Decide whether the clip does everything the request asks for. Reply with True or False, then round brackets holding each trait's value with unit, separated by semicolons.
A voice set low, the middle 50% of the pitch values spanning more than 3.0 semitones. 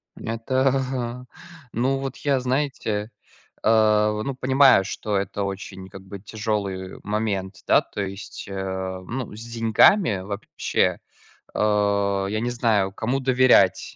True (110 Hz; 4.1 semitones)